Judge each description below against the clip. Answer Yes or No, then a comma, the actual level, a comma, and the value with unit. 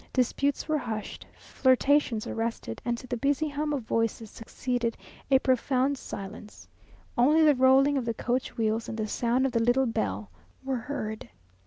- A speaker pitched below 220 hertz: No, very high, 250 Hz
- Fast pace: No, average, 165 wpm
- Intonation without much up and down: No, average, 3.2 semitones